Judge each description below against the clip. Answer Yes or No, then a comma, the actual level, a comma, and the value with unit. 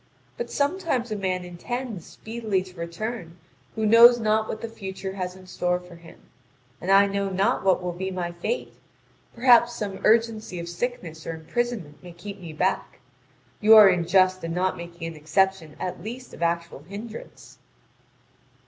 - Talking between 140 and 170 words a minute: Yes, average, 165 wpm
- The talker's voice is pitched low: No, high, 190 Hz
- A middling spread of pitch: Yes, average, 4.2 semitones